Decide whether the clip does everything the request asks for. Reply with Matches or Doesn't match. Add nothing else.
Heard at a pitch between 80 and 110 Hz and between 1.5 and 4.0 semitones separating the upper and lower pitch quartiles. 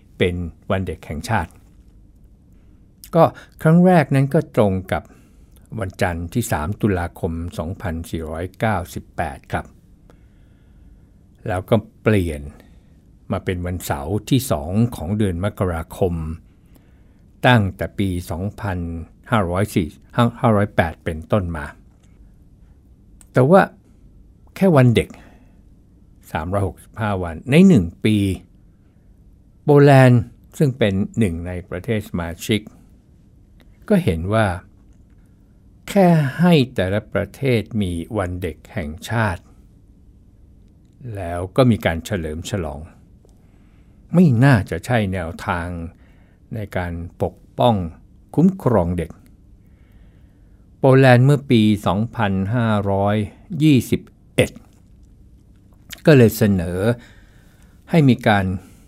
Matches